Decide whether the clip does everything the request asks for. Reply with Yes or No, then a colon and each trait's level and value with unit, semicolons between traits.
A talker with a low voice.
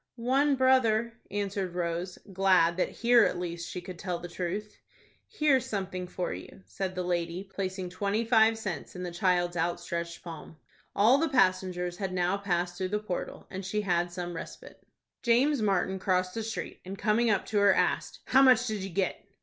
No: high, 190 Hz